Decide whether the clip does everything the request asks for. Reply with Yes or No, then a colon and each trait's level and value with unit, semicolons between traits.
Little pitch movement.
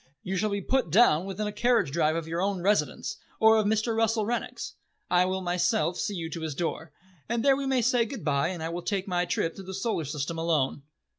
No: average, 5.0 semitones